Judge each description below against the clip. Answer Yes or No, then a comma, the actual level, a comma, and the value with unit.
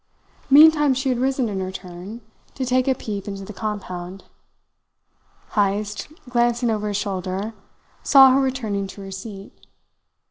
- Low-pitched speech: No, high, 210 Hz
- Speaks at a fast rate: No, average, 145 wpm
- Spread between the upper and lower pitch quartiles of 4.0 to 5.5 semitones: Yes, average, 4.7 semitones